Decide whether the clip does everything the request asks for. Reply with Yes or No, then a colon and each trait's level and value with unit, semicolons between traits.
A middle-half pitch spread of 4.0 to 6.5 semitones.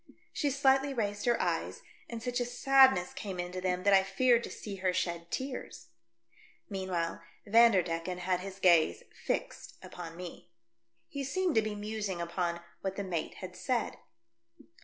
Yes: average, 5.1 semitones